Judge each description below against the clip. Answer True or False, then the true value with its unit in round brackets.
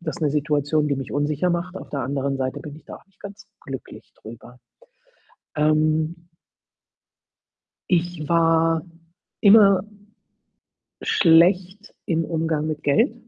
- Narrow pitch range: False (3.2 semitones)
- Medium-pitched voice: True (160 Hz)